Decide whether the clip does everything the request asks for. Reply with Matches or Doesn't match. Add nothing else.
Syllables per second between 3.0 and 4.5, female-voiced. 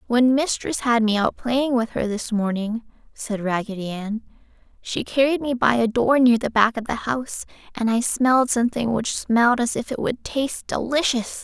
Doesn't match